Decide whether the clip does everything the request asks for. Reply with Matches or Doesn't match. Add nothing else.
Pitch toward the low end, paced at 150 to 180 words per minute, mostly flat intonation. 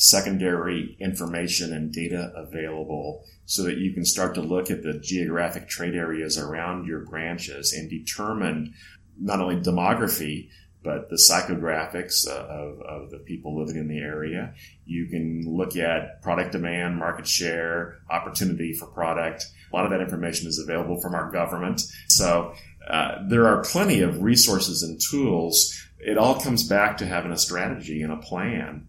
Matches